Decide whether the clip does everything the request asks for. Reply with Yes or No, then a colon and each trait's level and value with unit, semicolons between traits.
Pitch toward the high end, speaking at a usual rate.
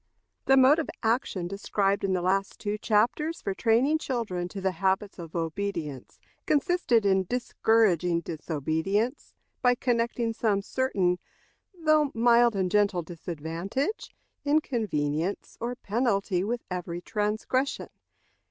No: high, 205 Hz; slow, 115 wpm